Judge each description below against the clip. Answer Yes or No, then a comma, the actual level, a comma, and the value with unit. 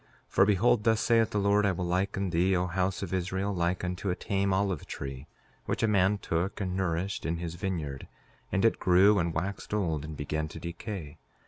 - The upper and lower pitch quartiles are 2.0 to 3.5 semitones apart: Yes, average, 2.8 semitones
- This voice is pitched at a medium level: No, very low, 95 Hz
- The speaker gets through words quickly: Yes, fast, 210 wpm